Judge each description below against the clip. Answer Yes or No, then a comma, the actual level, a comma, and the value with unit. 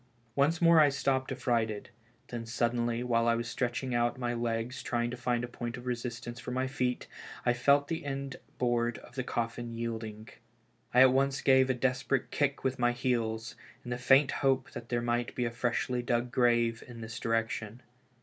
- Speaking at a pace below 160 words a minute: No, average, 190 wpm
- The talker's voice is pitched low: Yes, low, 120 Hz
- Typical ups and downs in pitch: No, narrow, 1.7 semitones